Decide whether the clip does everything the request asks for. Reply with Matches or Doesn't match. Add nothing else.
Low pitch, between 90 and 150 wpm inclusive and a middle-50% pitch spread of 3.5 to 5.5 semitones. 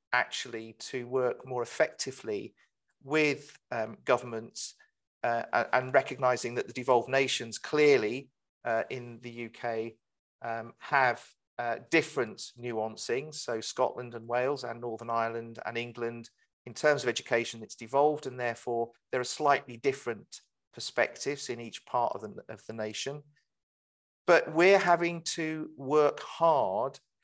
Doesn't match